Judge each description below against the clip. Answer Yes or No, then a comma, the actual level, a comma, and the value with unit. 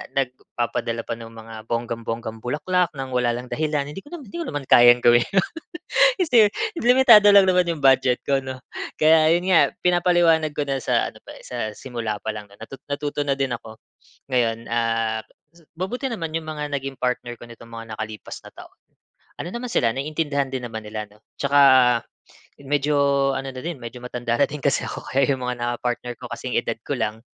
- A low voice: Yes, low, 130 Hz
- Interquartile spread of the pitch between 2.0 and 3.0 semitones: No, average, 4.7 semitones